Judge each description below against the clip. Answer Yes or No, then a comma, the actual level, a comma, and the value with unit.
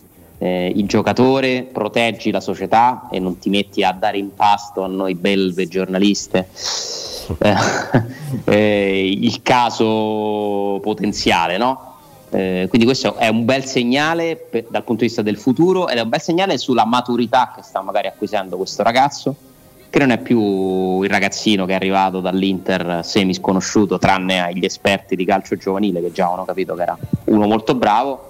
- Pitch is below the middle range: Yes, low, 105 Hz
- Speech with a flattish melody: No, average, 4.1 semitones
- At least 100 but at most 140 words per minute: No, average, 160 wpm